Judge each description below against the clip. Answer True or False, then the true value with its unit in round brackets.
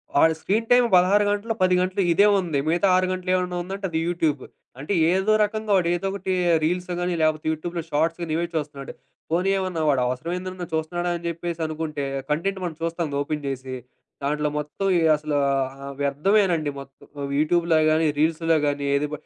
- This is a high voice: False (170 Hz)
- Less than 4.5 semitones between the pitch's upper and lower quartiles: True (3.4 semitones)